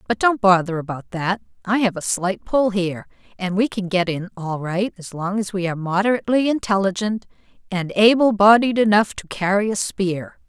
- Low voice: No, high, 200 Hz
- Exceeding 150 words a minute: Yes, average, 190 wpm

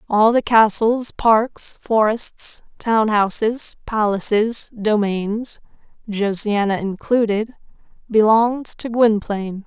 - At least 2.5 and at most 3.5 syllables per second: Yes, 3.4 syllables/s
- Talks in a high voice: Yes, high, 220 Hz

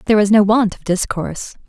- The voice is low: No, high, 205 Hz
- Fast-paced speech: Yes, fast, 215 wpm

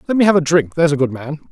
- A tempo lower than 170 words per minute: No, fast, 360 wpm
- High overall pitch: No, medium, 155 Hz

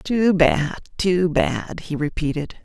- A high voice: No, medium, 170 Hz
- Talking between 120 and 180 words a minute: Yes, slow, 135 wpm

